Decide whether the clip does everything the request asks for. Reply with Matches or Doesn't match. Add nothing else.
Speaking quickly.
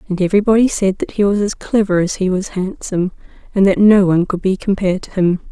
Matches